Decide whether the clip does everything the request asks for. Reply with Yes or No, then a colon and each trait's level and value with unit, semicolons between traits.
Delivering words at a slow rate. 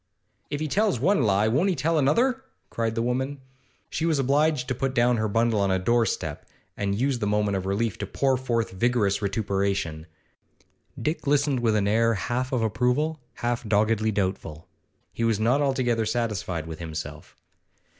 No: average, 175 wpm